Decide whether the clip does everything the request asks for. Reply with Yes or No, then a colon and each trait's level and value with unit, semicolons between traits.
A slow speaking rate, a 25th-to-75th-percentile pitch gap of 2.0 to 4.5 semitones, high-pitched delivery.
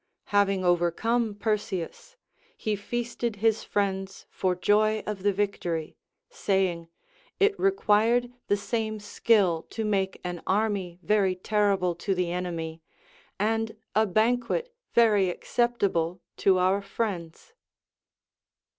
Yes: slow, 110 wpm; average, 3.3 semitones; high, 205 Hz